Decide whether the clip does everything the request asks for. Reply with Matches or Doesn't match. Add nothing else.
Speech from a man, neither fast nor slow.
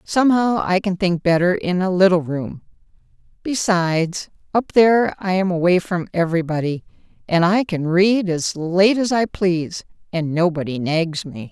Doesn't match